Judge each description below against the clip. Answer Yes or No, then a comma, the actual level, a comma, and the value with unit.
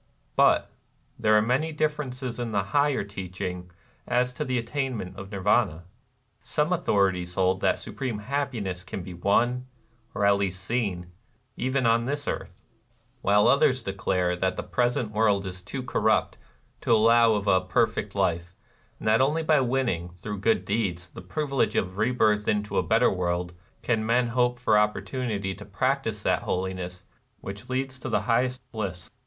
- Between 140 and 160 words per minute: No, average, 170 wpm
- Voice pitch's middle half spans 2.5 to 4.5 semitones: No, average, 5.0 semitones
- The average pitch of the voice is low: Yes, low, 105 Hz